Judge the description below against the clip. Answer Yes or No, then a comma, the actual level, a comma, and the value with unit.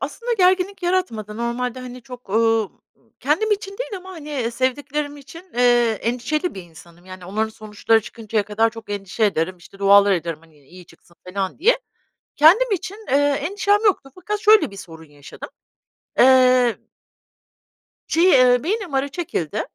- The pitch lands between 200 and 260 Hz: Yes, high, 245 Hz